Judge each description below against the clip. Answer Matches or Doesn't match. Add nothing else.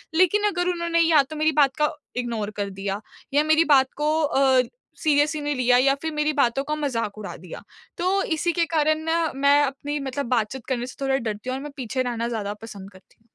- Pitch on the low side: Doesn't match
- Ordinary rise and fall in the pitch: Matches